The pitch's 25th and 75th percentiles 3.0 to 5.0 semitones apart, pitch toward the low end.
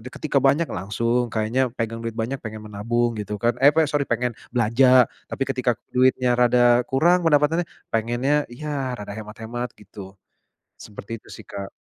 Yes: average, 3.3 semitones; low, 120 Hz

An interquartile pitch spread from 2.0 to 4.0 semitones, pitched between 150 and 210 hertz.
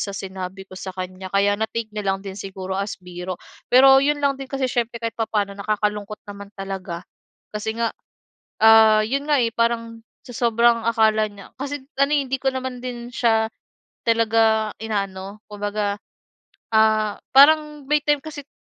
No: average, 3.7 semitones; high, 220 Hz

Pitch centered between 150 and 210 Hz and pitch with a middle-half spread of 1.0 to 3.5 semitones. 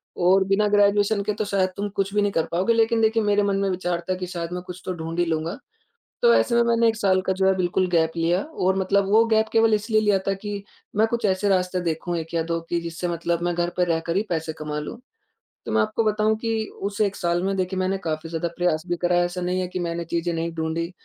Yes: medium, 185 Hz; average, 3.2 semitones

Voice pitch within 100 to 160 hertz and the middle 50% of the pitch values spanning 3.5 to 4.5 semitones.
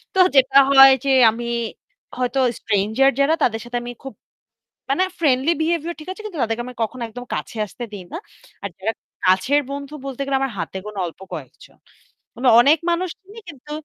No: very high, 270 Hz; average, 4.1 semitones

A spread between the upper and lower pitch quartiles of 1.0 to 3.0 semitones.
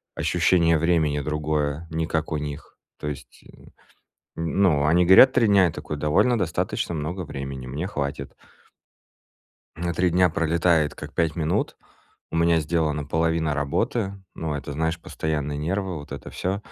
Yes: average, 2.7 semitones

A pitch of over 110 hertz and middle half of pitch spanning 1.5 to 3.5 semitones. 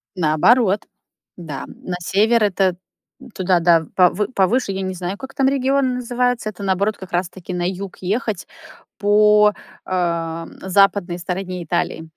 Yes: high, 190 Hz; average, 3.2 semitones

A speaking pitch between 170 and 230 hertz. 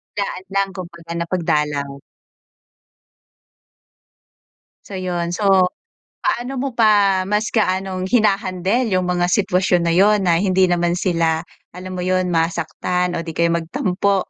Yes: medium, 185 Hz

